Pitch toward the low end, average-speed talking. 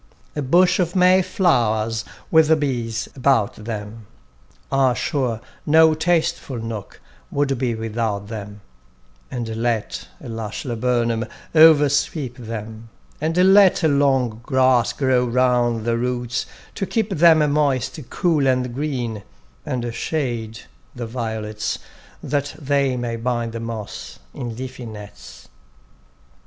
No: low, 125 Hz; slow, 120 wpm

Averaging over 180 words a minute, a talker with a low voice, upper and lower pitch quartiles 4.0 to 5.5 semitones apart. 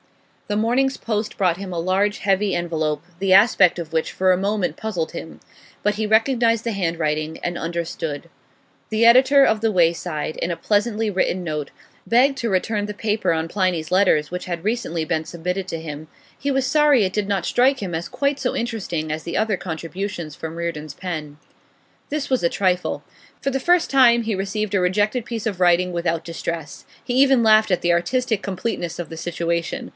No: average, 190 wpm; high, 190 Hz; average, 4.8 semitones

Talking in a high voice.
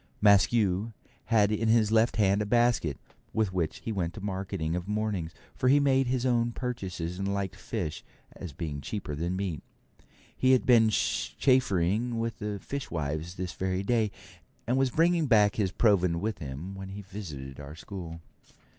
No: low, 100 Hz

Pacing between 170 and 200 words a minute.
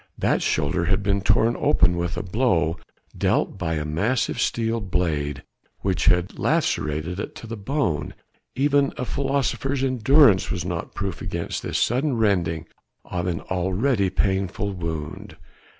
No: average, 145 wpm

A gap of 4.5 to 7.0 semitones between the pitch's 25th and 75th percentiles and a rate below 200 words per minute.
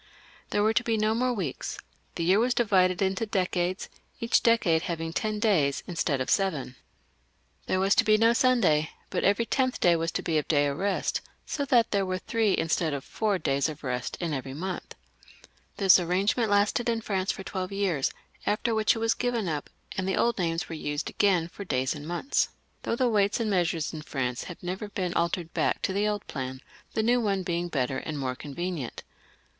No: average, 4.9 semitones; fast, 205 wpm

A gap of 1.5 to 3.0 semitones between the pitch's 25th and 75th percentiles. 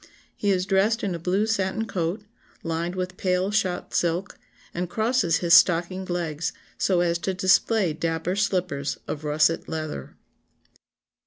Yes: narrow, 2.6 semitones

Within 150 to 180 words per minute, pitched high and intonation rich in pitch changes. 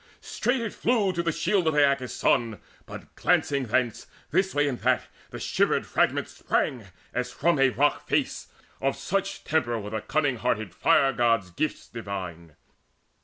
No: average, 165 wpm; low, 135 Hz; wide, 6.0 semitones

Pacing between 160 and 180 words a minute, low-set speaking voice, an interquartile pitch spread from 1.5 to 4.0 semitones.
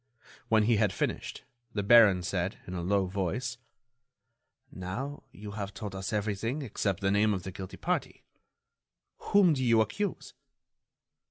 No: average, 150 wpm; low, 105 Hz; average, 3.3 semitones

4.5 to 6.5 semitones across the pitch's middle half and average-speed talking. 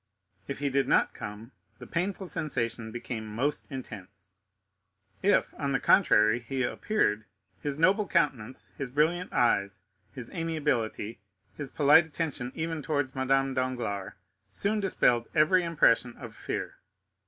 No: wide, 5.6 semitones; slow, 130 wpm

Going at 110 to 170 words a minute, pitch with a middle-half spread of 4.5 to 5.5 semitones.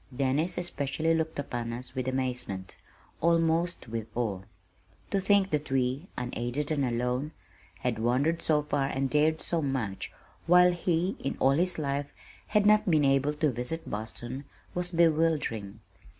Yes: average, 150 wpm; average, 4.8 semitones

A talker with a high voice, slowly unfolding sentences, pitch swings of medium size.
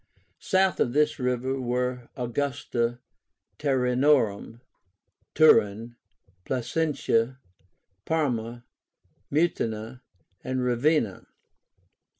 No: low, 125 Hz; slow, 65 wpm; average, 3.3 semitones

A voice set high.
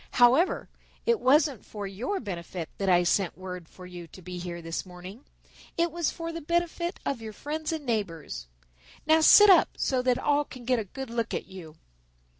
Yes: high, 235 Hz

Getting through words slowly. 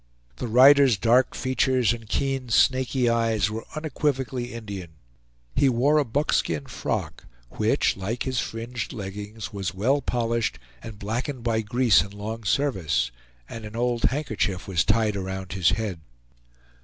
No: average, 145 wpm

